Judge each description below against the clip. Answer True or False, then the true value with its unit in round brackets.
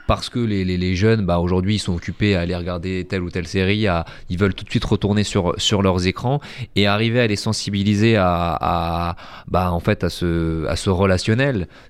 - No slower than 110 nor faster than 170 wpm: False (220 wpm)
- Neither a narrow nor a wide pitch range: True (3.0 semitones)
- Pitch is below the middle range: True (95 Hz)